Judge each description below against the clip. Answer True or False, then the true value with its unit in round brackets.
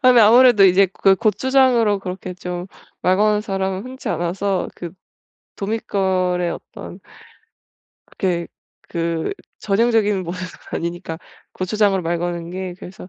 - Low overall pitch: False (190 Hz)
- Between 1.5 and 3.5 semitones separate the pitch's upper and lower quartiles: True (2.9 semitones)